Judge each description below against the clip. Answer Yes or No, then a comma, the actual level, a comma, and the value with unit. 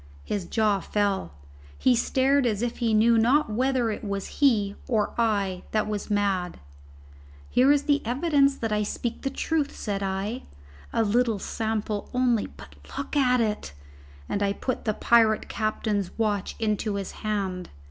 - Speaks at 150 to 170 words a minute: Yes, average, 160 wpm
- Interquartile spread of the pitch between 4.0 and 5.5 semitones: No, average, 3.3 semitones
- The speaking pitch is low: No, high, 220 Hz